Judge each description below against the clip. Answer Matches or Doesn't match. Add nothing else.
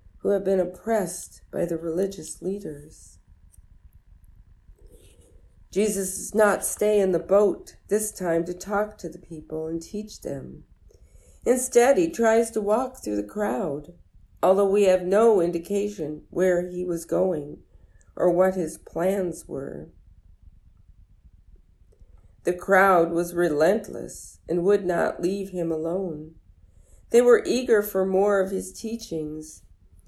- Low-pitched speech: Doesn't match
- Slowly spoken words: Matches